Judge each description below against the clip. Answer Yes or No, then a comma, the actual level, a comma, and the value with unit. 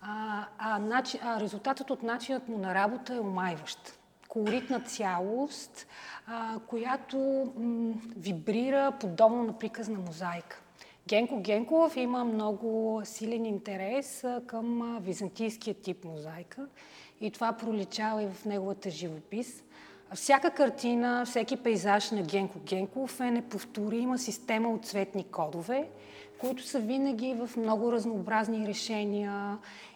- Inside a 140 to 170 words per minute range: No, slow, 115 wpm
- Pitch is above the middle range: Yes, high, 225 Hz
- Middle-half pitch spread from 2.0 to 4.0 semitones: Yes, average, 3.3 semitones